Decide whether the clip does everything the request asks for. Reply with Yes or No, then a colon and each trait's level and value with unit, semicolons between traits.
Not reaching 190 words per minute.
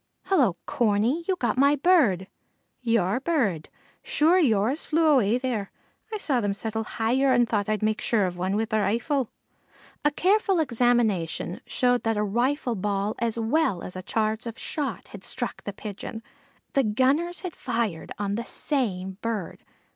Yes: average, 165 wpm